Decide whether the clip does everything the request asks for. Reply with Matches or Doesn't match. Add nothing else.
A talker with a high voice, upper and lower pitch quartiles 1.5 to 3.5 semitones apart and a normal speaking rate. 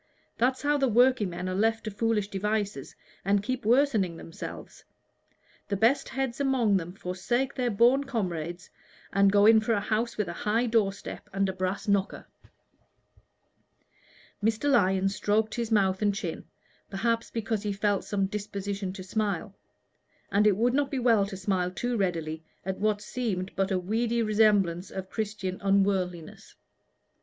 Matches